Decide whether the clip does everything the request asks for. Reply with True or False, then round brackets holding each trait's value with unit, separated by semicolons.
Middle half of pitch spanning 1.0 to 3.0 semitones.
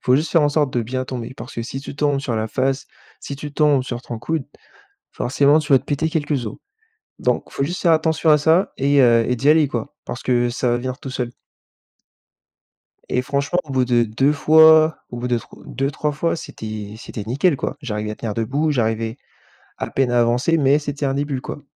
False (3.6 semitones)